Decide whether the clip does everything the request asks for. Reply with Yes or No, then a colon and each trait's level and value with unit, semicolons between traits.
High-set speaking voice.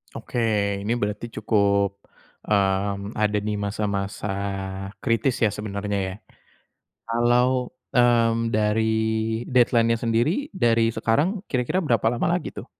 No: low, 115 Hz